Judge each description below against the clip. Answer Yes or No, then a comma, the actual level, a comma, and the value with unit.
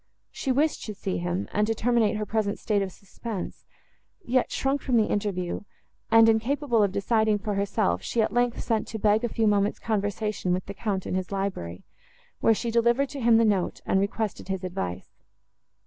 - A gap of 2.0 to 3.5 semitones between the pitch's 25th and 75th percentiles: Yes, average, 2.9 semitones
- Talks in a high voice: Yes, high, 210 Hz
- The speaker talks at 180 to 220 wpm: Yes, average, 195 wpm